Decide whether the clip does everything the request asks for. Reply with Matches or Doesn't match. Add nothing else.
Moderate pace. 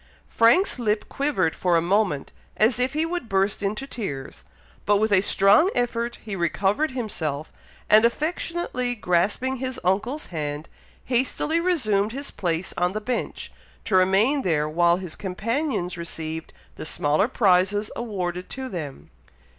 Matches